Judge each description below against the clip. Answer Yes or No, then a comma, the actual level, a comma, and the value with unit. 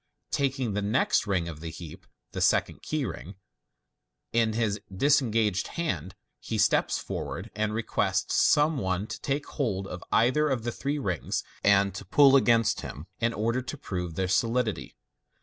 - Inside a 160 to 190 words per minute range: Yes, average, 165 wpm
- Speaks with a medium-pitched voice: No, low, 110 Hz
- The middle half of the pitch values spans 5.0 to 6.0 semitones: Yes, wide, 5.5 semitones